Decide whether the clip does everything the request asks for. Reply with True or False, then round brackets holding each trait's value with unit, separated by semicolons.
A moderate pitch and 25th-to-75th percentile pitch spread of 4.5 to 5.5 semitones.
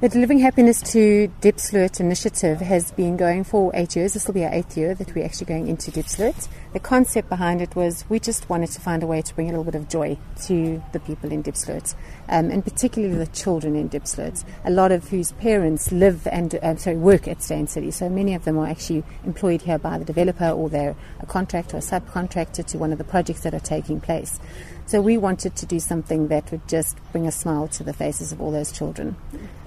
False (170 Hz; 3.1 semitones)